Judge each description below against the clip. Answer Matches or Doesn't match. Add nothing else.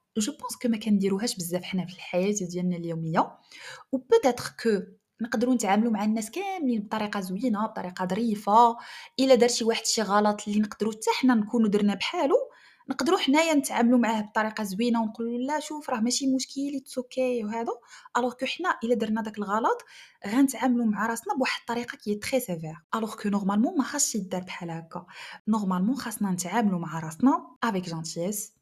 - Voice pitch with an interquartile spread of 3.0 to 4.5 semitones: Matches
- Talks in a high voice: Matches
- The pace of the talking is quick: Matches